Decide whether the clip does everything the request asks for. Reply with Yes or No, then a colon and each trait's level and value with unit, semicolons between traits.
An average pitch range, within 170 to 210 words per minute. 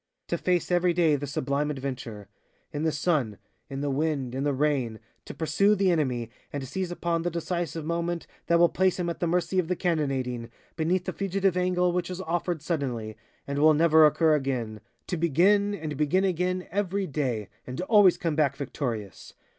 Yes: average, 4.4 semitones; average, 190 wpm